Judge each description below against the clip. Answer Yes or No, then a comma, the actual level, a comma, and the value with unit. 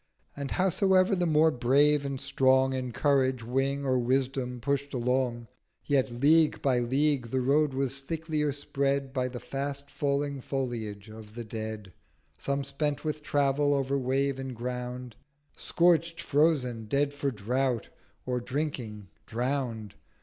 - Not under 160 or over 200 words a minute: No, average, 140 wpm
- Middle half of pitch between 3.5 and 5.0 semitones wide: No, narrow, 2.5 semitones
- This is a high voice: No, low, 135 Hz